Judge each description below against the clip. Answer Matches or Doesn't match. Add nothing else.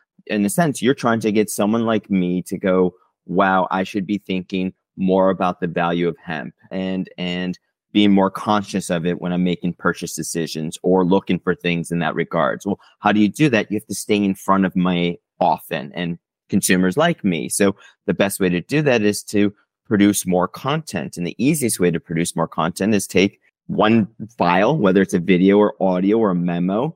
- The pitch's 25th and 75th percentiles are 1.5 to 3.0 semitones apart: Matches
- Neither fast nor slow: Doesn't match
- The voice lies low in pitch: Matches